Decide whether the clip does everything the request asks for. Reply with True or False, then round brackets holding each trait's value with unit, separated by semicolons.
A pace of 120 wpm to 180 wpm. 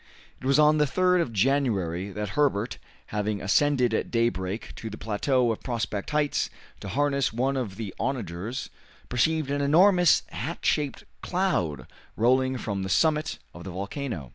True (160 wpm)